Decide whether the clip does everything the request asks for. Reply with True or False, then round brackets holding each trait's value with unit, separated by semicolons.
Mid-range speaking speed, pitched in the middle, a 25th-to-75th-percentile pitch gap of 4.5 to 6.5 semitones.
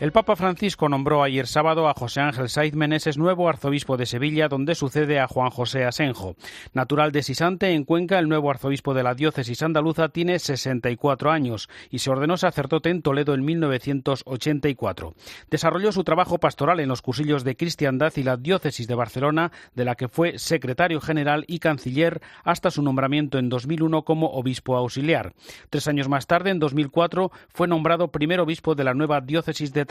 False (180 wpm; 150 Hz; 3.5 semitones)